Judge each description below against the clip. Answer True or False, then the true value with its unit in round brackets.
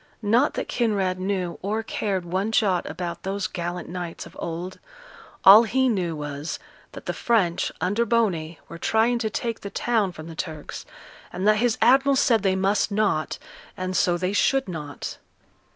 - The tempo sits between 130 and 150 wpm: False (170 wpm)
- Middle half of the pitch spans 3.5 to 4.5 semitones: True (4.2 semitones)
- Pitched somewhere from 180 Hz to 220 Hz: True (190 Hz)